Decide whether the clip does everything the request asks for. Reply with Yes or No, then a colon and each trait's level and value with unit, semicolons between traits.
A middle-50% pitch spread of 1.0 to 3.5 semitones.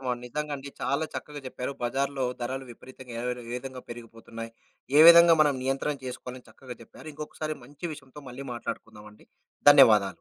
Yes: average, 2.8 semitones